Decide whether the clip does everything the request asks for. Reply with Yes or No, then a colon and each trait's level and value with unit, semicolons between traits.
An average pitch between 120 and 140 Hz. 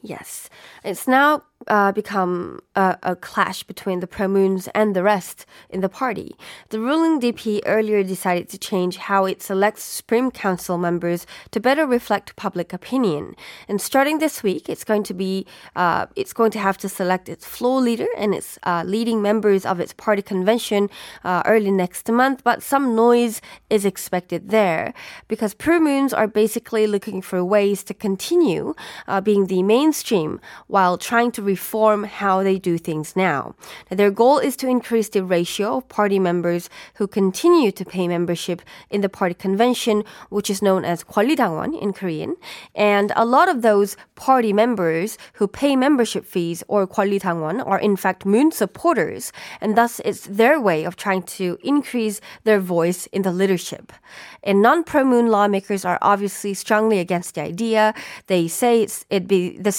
No: high, 205 Hz